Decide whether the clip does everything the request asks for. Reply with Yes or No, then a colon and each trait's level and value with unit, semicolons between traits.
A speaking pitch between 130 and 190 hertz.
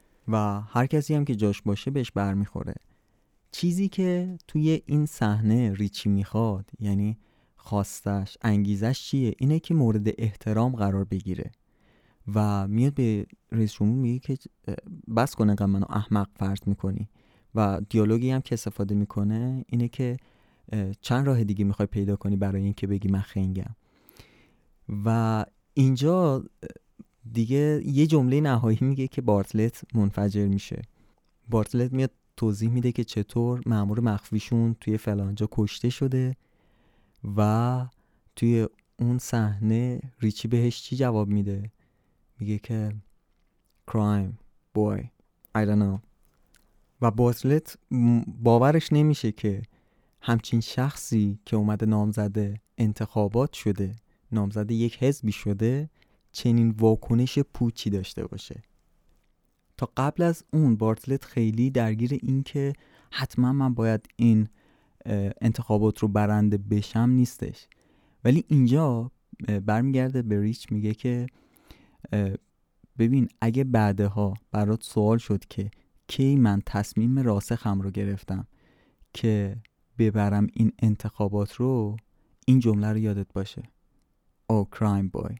No: low, 110 Hz